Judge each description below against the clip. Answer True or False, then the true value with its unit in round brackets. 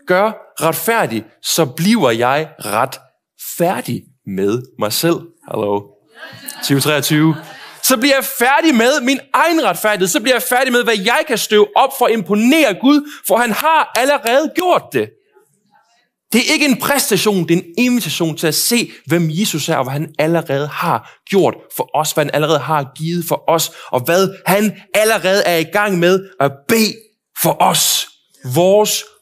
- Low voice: False (190 Hz)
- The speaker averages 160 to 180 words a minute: True (170 wpm)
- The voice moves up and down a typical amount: False (7.4 semitones)